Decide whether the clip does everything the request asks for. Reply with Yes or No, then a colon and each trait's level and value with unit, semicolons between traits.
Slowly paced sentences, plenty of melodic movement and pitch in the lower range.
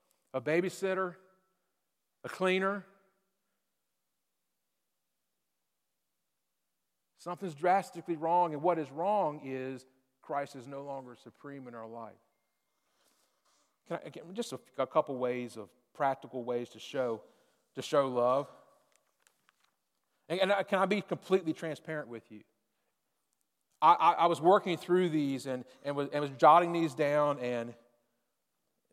No: slow, 130 wpm; wide, 6.4 semitones; medium, 145 Hz